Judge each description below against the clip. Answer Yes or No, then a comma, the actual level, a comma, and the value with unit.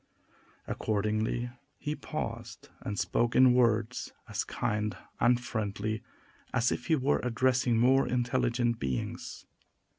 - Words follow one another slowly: Yes, slow, 115 wpm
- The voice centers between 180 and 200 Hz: No, low, 120 Hz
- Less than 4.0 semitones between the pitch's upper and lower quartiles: Yes, narrow, 2.6 semitones